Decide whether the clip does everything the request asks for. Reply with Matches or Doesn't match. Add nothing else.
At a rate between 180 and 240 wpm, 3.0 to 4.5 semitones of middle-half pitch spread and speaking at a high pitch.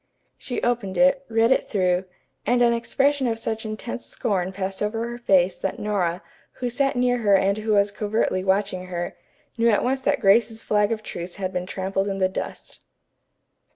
Matches